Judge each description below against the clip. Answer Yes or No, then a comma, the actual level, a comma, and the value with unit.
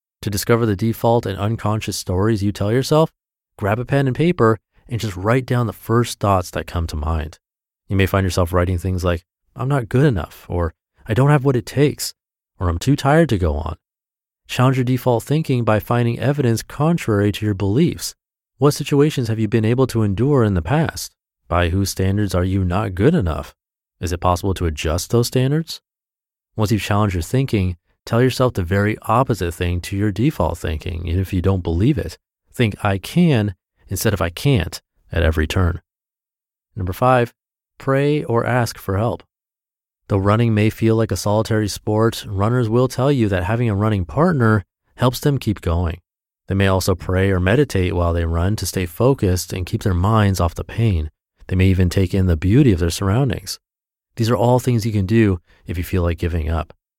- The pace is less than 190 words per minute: No, average, 200 wpm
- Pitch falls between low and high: No, low, 105 Hz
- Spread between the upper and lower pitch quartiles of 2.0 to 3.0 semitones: No, average, 4.9 semitones